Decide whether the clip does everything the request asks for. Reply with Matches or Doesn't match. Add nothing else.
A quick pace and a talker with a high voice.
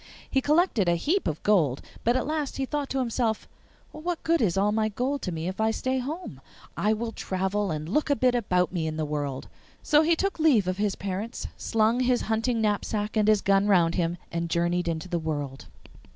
Matches